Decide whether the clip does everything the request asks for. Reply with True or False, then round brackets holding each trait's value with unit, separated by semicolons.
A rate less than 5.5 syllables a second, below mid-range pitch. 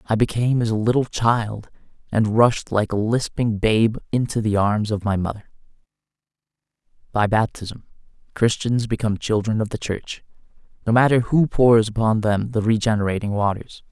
True (5.1 syllables/s; 110 Hz)